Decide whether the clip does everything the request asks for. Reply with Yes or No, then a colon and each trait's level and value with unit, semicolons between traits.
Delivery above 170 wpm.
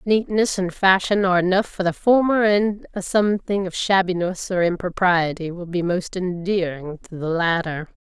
No: average, 165 wpm